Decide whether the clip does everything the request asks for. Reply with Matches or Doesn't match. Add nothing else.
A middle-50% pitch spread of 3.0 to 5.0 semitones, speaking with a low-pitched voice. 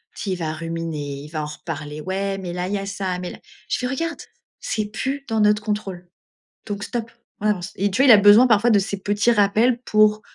Doesn't match